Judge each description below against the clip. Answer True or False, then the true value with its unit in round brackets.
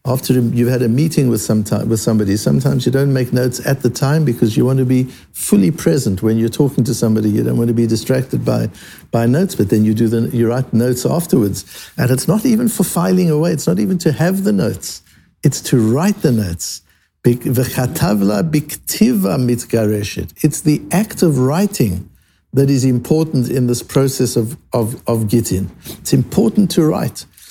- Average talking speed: True (180 wpm)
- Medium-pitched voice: False (125 Hz)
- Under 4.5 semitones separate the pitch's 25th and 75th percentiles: False (5.2 semitones)